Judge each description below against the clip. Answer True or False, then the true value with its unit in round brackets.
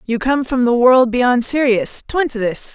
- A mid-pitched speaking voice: False (250 Hz)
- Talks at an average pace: False (220 wpm)